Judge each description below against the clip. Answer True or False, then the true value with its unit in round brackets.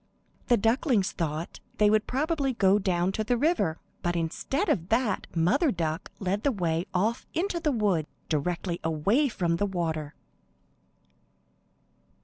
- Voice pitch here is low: False (195 Hz)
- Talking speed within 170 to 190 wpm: False (140 wpm)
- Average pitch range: False (6.5 semitones)